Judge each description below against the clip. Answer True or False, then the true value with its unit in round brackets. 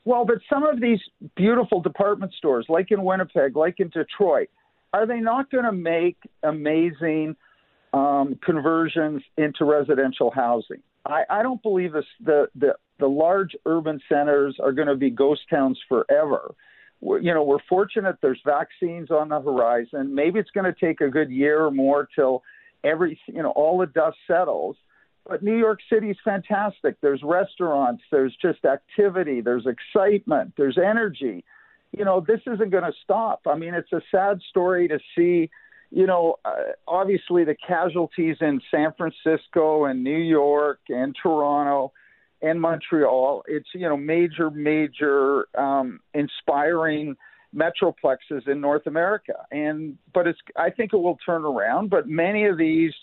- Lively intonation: False (5.0 semitones)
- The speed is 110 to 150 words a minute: False (160 wpm)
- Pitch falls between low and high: True (165 Hz)